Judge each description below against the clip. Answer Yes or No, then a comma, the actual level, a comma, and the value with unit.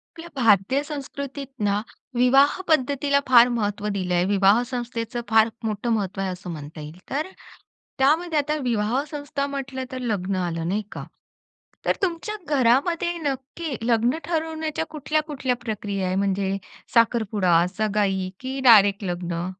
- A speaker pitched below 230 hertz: No, high, 235 Hz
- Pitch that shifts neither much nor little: No, wide, 6.1 semitones